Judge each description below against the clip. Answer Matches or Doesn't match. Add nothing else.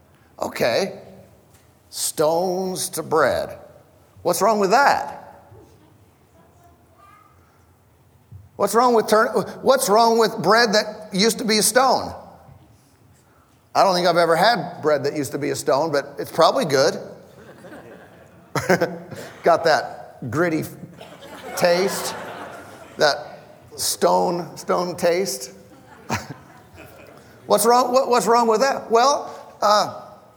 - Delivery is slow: Matches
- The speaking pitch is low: Doesn't match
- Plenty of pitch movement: Matches